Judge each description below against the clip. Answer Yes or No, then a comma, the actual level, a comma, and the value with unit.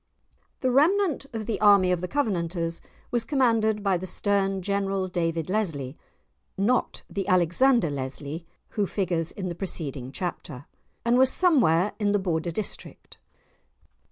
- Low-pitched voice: No, high, 195 Hz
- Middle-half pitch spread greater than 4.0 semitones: Yes, average, 4.6 semitones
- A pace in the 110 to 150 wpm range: Yes, average, 140 wpm